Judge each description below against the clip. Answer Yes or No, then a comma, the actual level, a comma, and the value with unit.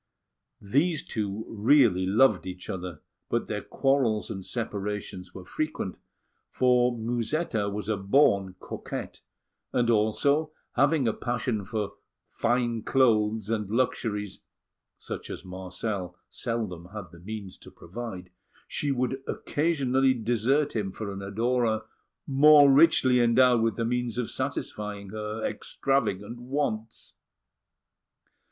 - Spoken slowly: Yes, slow, 120 wpm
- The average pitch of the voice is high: No, low, 110 Hz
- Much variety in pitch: No, average, 3.9 semitones